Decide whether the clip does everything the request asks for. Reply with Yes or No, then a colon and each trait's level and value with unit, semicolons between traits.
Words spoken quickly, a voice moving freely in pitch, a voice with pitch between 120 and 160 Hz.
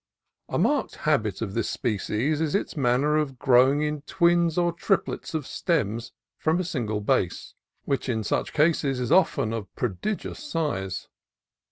No: average, 160 wpm; wide, 6.3 semitones; medium, 140 Hz